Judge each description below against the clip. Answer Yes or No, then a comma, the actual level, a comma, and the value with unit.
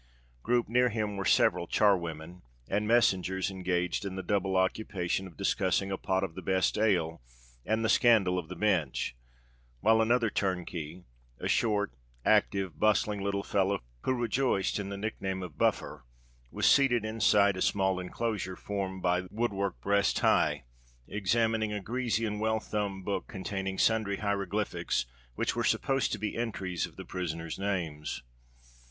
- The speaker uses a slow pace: No, average, 155 wpm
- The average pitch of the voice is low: Yes, low, 100 Hz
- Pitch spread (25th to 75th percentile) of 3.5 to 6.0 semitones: No, average, 2.9 semitones